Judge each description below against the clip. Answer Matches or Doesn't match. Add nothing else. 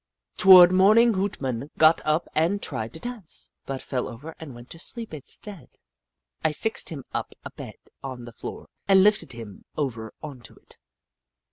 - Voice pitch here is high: Doesn't match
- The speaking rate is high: Doesn't match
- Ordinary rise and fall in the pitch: Doesn't match